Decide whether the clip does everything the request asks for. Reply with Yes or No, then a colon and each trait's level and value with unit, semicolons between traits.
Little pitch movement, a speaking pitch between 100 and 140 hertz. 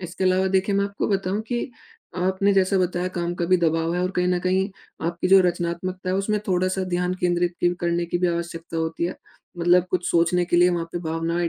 No: narrow, 1.4 semitones; medium, 180 Hz